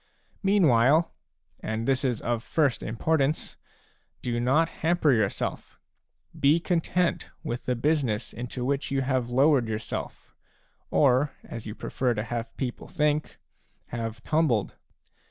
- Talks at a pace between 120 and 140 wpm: Yes, slow, 135 wpm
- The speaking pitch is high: No, low, 130 Hz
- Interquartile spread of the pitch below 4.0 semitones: No, average, 4.4 semitones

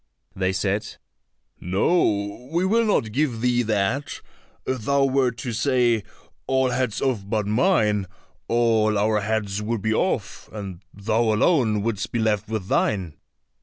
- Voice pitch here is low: Yes, low, 110 Hz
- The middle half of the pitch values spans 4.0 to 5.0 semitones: No, average, 3.5 semitones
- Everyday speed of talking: Yes, average, 145 wpm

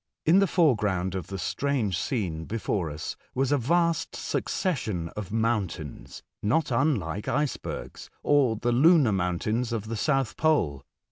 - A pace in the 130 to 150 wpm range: Yes, average, 140 wpm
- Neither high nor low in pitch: No, low, 115 Hz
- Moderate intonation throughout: No, wide, 7.1 semitones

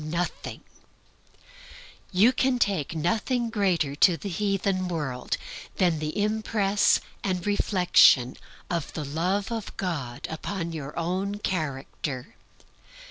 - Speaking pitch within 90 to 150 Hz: No, medium, 180 Hz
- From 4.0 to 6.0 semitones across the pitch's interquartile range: Yes, average, 4.6 semitones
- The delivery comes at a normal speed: No, slow, 105 wpm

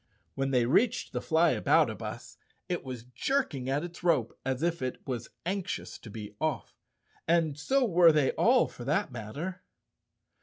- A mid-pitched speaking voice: Yes, medium, 155 Hz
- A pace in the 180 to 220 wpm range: No, average, 155 wpm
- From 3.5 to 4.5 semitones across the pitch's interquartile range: No, wide, 5.6 semitones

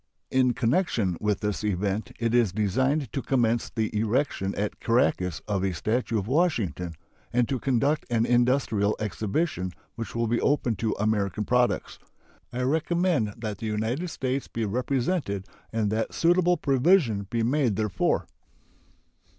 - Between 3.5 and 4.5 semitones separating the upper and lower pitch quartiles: Yes, average, 4.1 semitones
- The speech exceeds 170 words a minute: No, average, 145 wpm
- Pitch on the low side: Yes, low, 115 Hz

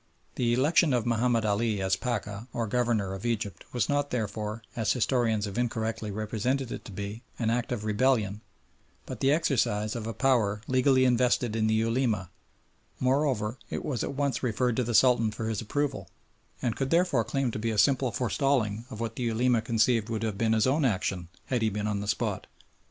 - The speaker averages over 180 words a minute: Yes, average, 195 wpm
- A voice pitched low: Yes, low, 115 Hz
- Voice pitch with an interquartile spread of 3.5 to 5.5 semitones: No, average, 3.0 semitones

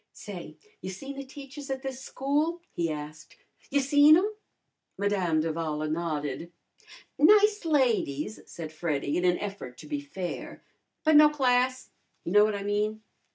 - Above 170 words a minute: No, average, 155 wpm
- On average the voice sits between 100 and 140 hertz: No, high, 215 Hz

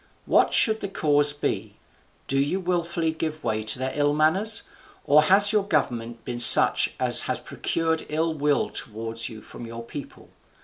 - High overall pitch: No, medium, 150 Hz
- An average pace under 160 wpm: No, average, 170 wpm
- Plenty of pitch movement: Yes, wide, 5.9 semitones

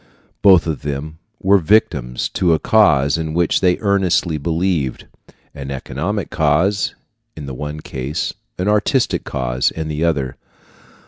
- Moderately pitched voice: No, very low, 80 Hz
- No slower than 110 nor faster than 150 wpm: Yes, average, 140 wpm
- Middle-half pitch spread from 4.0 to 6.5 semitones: Yes, average, 4.9 semitones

